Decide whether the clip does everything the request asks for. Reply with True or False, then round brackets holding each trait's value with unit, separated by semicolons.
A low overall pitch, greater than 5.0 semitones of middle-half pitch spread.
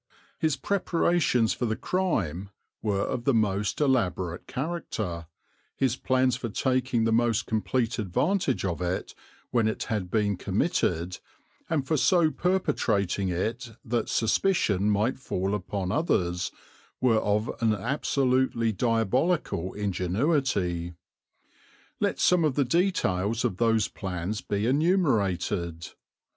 True (115 Hz; 5.4 semitones)